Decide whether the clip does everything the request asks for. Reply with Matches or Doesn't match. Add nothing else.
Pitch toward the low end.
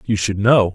Matches